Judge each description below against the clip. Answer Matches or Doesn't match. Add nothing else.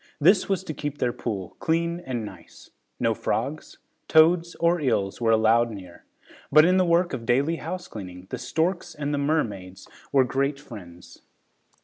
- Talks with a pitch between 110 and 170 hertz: Matches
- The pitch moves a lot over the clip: Matches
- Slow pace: Doesn't match